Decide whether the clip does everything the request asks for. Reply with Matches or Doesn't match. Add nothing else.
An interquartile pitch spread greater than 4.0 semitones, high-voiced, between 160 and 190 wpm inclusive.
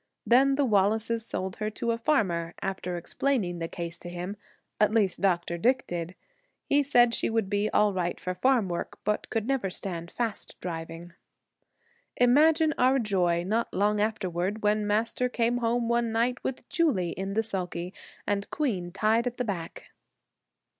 Matches